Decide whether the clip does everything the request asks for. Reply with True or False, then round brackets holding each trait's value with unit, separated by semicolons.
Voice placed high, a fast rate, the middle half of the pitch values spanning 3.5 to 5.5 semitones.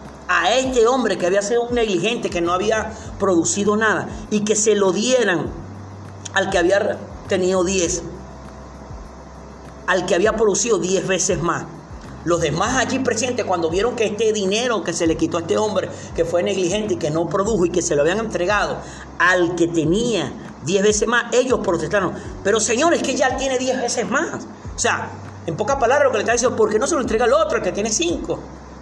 True (195 Hz; 205 wpm; 4.9 semitones)